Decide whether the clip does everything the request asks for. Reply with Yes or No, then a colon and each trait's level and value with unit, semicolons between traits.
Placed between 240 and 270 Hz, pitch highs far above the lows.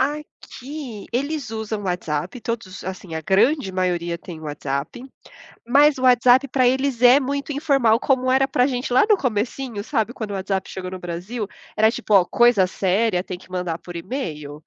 No: high, 220 Hz; wide, 6.0 semitones